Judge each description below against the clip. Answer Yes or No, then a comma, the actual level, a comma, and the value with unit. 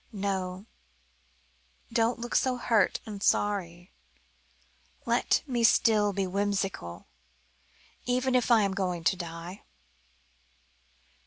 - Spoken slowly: Yes, slow, 100 wpm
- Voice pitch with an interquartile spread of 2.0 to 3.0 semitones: No, average, 3.9 semitones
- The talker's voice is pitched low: No, high, 200 Hz